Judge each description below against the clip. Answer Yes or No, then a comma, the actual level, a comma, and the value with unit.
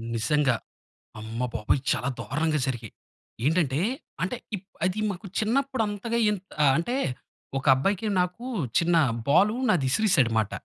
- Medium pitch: Yes, medium, 165 Hz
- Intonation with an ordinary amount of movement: No, wide, 7.9 semitones